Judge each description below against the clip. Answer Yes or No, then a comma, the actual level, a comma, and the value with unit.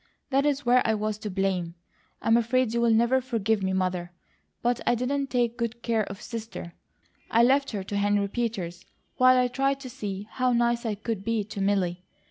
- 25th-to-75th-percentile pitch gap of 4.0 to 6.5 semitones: No, average, 3.6 semitones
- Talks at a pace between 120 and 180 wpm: No, average, 195 wpm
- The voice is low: No, high, 225 Hz